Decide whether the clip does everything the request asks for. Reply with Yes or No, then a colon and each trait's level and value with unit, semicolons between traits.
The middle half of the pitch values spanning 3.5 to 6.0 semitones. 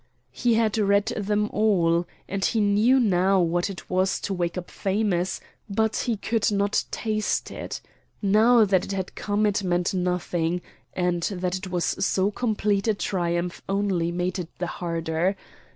No: average, 2.9 semitones